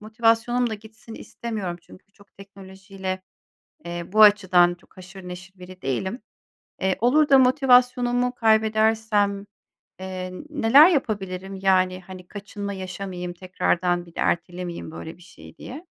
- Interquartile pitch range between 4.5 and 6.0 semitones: No, average, 3.5 semitones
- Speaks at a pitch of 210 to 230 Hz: No, high, 195 Hz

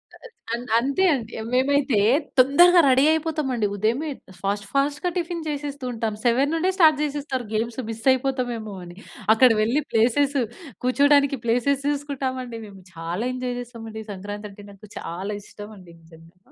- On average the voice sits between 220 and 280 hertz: Yes, very high, 250 Hz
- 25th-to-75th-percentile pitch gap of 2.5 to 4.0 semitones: No, average, 4.8 semitones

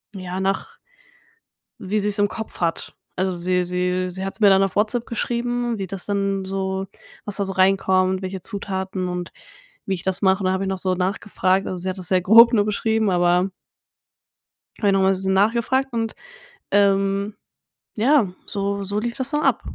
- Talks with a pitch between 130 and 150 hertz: No, high, 195 Hz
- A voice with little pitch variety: Yes, narrow, 1.9 semitones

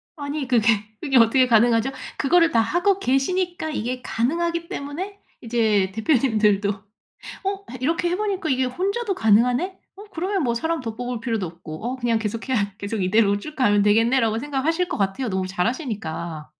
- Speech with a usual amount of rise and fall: No, wide, 6.8 semitones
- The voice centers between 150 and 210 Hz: No, very high, 250 Hz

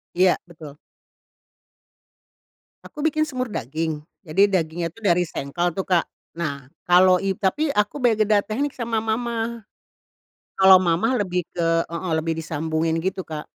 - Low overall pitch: No, medium, 185 Hz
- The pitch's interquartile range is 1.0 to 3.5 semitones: No, average, 5.0 semitones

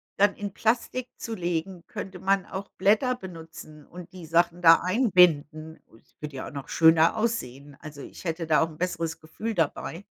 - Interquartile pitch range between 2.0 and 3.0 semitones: No, average, 3.6 semitones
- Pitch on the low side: No, medium, 175 Hz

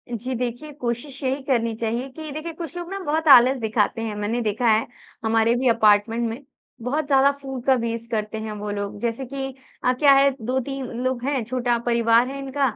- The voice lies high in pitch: Yes, high, 245 Hz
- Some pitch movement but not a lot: Yes, average, 3.1 semitones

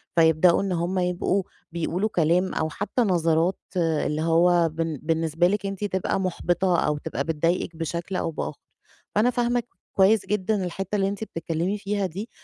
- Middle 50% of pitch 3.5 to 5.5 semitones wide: No, average, 3.1 semitones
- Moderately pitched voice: Yes, medium, 180 Hz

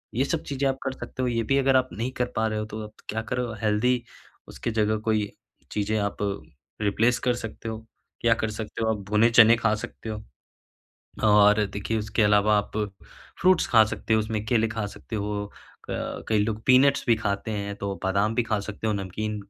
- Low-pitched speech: Yes, low, 110 Hz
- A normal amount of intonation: No, narrow, 2.1 semitones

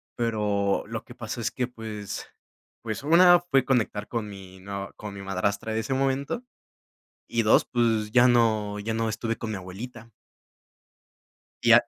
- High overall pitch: No, low, 110 Hz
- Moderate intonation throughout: Yes, average, 3.0 semitones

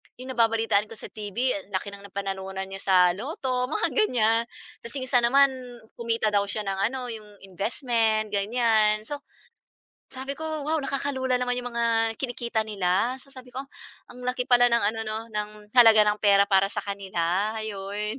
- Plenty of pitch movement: No, average, 3.6 semitones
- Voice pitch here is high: Yes, high, 220 Hz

